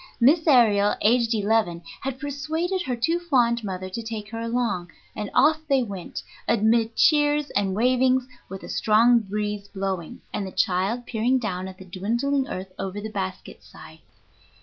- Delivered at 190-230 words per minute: No, average, 165 wpm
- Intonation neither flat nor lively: Yes, average, 4.5 semitones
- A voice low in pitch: No, high, 225 Hz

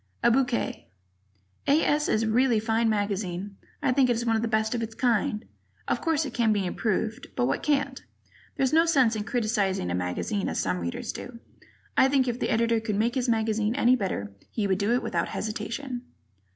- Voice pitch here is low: No, high, 225 Hz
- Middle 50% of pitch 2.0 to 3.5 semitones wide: Yes, average, 3.2 semitones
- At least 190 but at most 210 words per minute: Yes, fast, 205 wpm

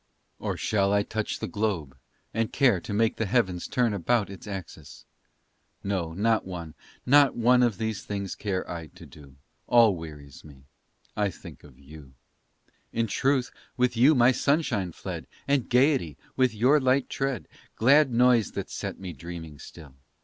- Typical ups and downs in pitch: No, wide, 6.4 semitones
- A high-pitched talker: No, low, 105 Hz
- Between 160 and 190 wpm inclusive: Yes, average, 165 wpm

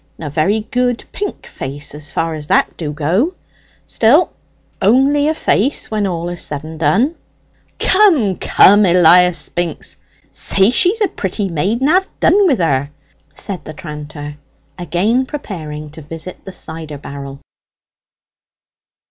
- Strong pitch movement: Yes, wide, 8.0 semitones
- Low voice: No, medium, 180 Hz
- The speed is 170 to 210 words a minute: No, average, 140 wpm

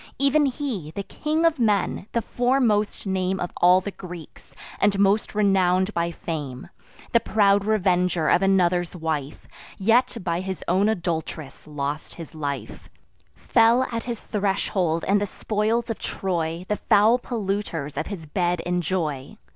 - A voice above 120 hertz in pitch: Yes, high, 190 Hz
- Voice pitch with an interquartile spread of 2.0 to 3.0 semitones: No, average, 4.1 semitones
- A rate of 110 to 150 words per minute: Yes, average, 145 wpm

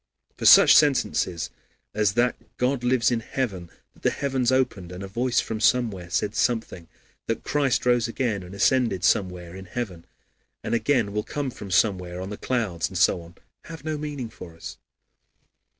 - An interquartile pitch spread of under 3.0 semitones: No, wide, 5.4 semitones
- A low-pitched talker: Yes, low, 110 Hz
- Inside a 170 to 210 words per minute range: Yes, average, 175 wpm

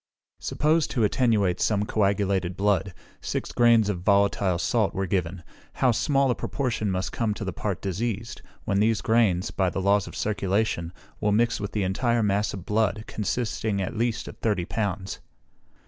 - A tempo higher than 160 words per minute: Yes, average, 170 wpm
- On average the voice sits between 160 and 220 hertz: No, low, 105 Hz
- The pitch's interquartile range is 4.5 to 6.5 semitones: No, average, 2.9 semitones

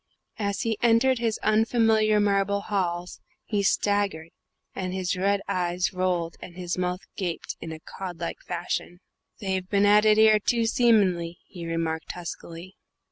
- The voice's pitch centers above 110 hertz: Yes, high, 190 Hz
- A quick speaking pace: No, average, 150 wpm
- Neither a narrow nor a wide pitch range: Yes, average, 3.2 semitones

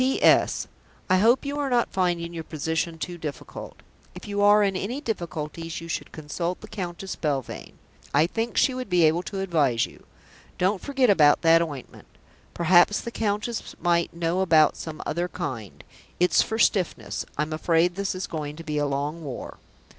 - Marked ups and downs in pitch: No, average, 4.2 semitones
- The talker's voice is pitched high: No, medium, 175 Hz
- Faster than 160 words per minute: Yes, average, 180 wpm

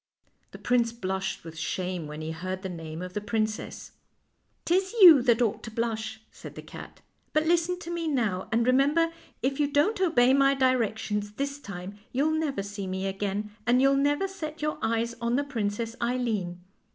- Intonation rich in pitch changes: Yes, wide, 6.2 semitones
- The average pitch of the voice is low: No, high, 235 Hz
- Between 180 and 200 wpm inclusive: Yes, average, 195 wpm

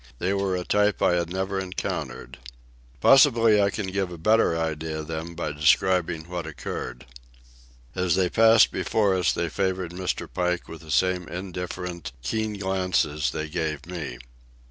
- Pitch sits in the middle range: No, very low, 90 Hz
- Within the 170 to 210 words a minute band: No, average, 160 wpm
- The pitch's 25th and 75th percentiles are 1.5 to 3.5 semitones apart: Yes, average, 2.9 semitones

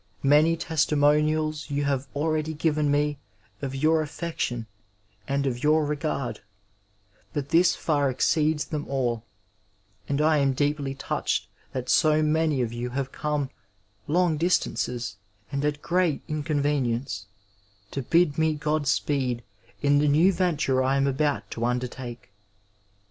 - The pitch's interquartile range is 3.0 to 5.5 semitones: No, narrow, 2.4 semitones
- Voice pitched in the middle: Yes, medium, 145 Hz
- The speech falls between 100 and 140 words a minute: Yes, slow, 135 wpm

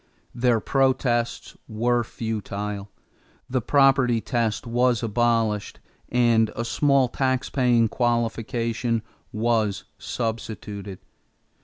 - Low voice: Yes, low, 115 Hz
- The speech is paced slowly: Yes, slow, 90 wpm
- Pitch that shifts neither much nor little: No, narrow, 1.9 semitones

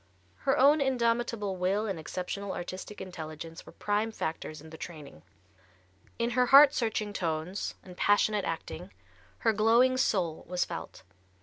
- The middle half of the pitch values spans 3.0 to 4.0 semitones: No, wide, 5.4 semitones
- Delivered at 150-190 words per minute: No, average, 140 wpm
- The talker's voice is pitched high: Yes, high, 200 Hz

